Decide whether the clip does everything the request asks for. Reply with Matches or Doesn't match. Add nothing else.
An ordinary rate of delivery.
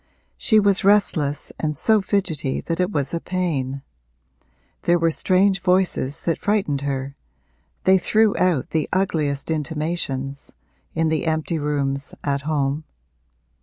Doesn't match